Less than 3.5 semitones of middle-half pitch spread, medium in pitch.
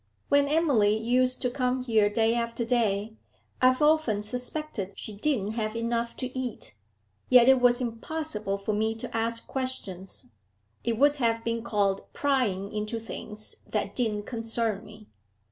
No: average, 3.1 semitones; high, 230 Hz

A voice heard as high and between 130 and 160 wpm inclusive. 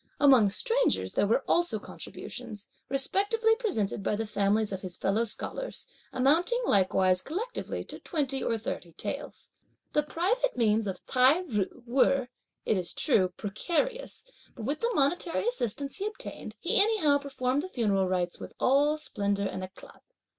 Yes: very high, 265 Hz; average, 155 wpm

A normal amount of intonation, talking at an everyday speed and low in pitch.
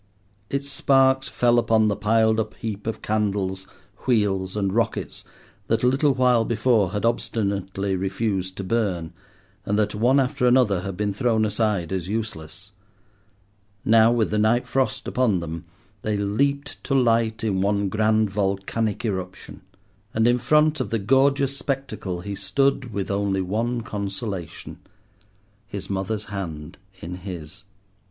Yes: average, 3.3 semitones; average, 145 wpm; low, 105 Hz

